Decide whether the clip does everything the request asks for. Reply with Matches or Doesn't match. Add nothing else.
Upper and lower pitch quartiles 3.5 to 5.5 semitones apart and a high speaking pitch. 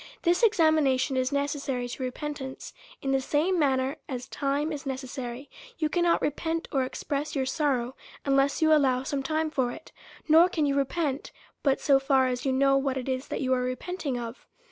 Doesn't match